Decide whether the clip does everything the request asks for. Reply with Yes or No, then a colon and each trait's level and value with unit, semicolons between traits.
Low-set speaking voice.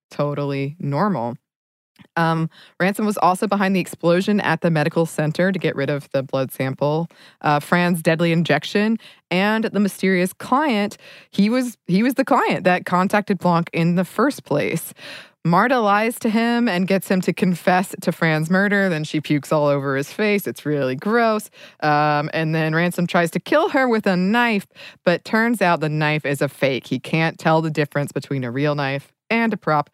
No: medium, 175 Hz